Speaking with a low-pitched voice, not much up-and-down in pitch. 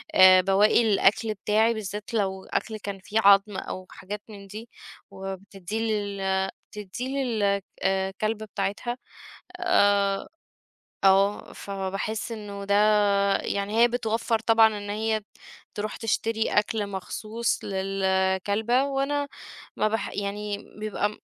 No: high, 205 Hz; narrow, 2.2 semitones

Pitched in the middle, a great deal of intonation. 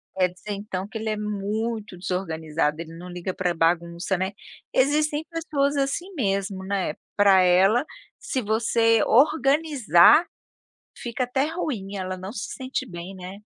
No: high, 205 Hz; wide, 6.0 semitones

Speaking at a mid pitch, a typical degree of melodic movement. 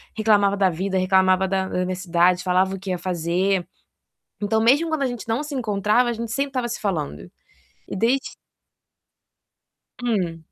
No: high, 195 Hz; average, 4.0 semitones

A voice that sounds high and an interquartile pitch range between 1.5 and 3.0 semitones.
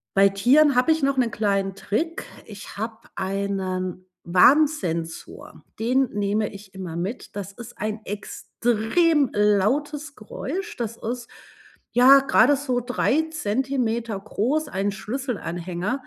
No: high, 220 Hz; wide, 5.4 semitones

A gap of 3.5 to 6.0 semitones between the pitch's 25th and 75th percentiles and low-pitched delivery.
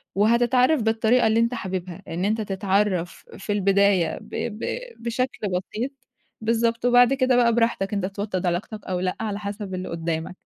No: average, 3.8 semitones; high, 210 Hz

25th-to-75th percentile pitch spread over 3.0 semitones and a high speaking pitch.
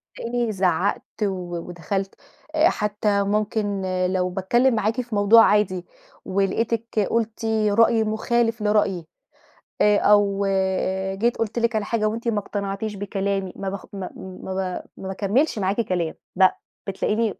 No: average, 2.7 semitones; high, 205 Hz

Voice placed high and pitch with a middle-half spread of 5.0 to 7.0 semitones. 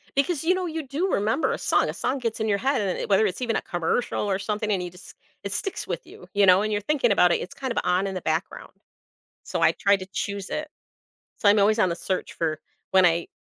Yes: high, 205 Hz; wide, 5.4 semitones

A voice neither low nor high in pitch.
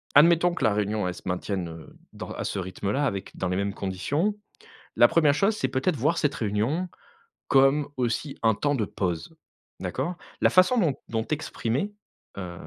No: low, 125 Hz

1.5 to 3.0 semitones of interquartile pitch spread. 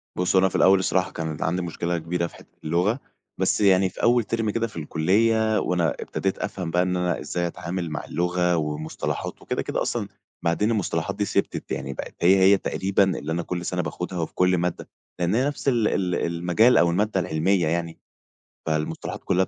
Yes: narrow, 2.5 semitones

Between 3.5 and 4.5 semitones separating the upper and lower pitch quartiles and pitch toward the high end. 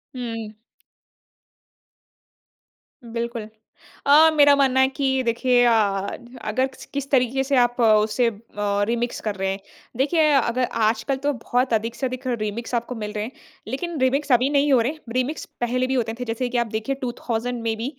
No: average, 2.7 semitones; high, 245 Hz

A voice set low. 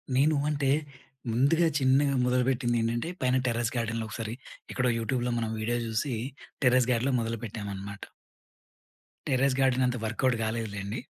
Yes: low, 120 Hz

